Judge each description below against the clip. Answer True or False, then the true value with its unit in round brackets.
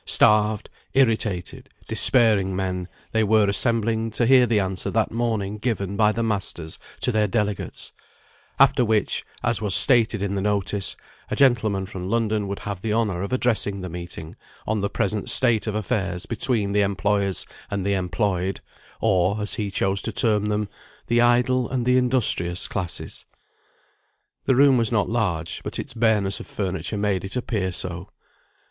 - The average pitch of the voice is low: True (105 Hz)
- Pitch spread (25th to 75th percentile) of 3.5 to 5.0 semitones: False (2.8 semitones)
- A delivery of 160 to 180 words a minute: True (165 wpm)